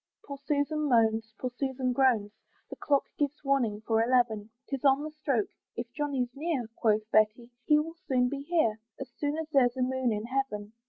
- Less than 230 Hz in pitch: No, very high, 255 Hz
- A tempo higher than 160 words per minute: Yes, average, 190 wpm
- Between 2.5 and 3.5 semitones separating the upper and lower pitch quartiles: No, average, 4.0 semitones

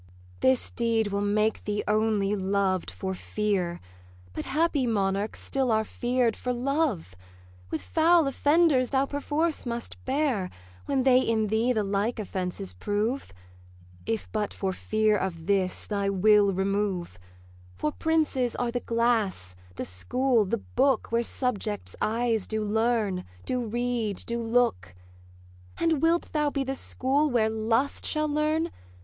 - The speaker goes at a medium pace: Yes, average, 145 wpm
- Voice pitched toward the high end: Yes, high, 225 Hz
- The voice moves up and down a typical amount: Yes, average, 4.5 semitones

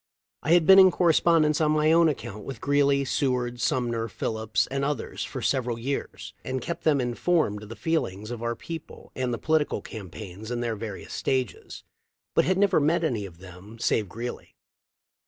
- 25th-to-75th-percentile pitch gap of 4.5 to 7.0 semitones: Yes, wide, 5.5 semitones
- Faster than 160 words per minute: Yes, average, 180 wpm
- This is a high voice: No, low, 125 Hz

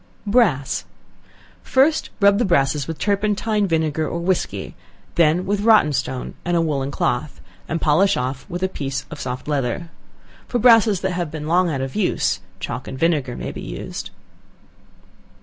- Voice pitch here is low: No, medium, 165 Hz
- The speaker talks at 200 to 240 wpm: No, average, 165 wpm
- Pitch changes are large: Yes, wide, 6.1 semitones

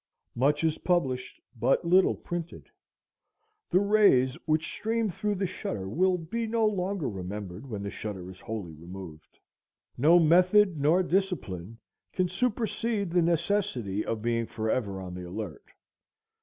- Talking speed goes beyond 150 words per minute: No, average, 140 wpm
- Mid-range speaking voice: Yes, medium, 155 Hz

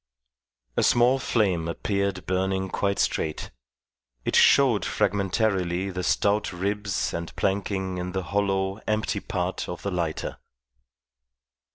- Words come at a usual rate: No, slow, 120 wpm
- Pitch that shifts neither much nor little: No, narrow, 2.0 semitones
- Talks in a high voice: No, very low, 95 Hz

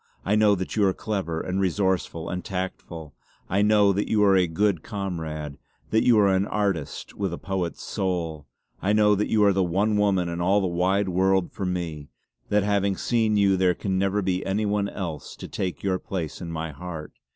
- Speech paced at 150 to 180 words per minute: No, fast, 205 wpm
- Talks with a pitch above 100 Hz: No, very low, 95 Hz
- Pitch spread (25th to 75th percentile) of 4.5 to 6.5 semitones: No, average, 2.8 semitones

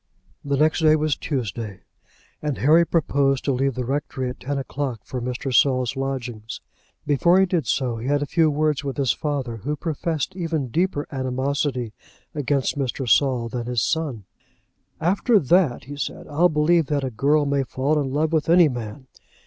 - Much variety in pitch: No, average, 3.2 semitones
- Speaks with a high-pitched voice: No, medium, 140 Hz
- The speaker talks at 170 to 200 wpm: Yes, average, 180 wpm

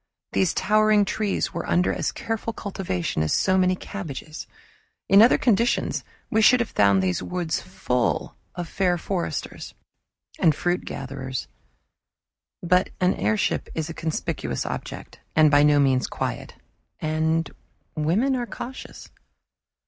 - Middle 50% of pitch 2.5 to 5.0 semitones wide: No, wide, 5.4 semitones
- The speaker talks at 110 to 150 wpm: Yes, slow, 135 wpm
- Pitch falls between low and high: Yes, medium, 175 Hz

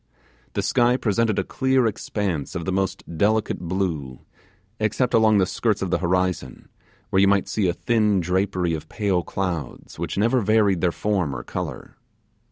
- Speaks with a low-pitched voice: Yes, very low, 95 Hz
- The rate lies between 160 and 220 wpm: Yes, average, 170 wpm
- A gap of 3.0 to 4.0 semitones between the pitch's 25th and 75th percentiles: Yes, average, 3.3 semitones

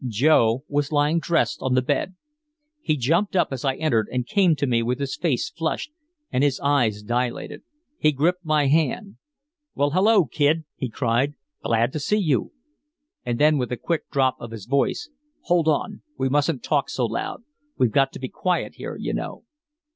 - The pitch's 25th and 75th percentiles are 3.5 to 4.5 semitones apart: Yes, average, 4.1 semitones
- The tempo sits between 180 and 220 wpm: Yes, average, 185 wpm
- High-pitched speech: No, medium, 140 Hz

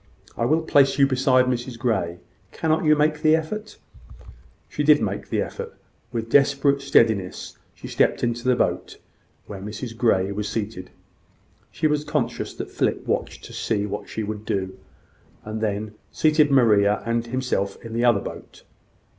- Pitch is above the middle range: No, low, 120 Hz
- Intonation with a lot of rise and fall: No, average, 4.9 semitones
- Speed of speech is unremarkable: Yes, average, 165 wpm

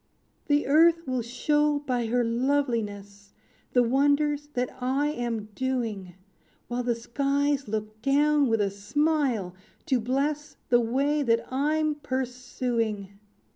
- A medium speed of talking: No, slow, 125 wpm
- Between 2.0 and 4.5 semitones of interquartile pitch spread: Yes, average, 4.0 semitones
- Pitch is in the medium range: No, very high, 255 Hz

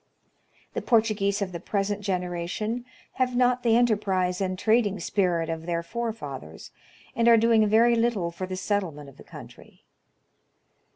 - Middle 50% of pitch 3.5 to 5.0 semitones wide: Yes, average, 4.3 semitones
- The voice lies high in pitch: Yes, high, 200 Hz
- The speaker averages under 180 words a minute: Yes, average, 150 wpm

